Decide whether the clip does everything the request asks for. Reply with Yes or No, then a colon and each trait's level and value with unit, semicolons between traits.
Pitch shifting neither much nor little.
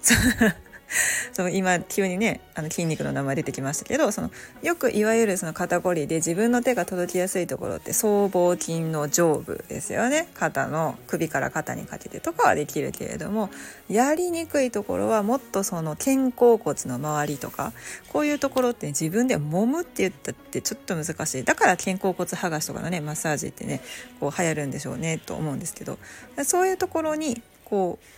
No: wide, 7.0 semitones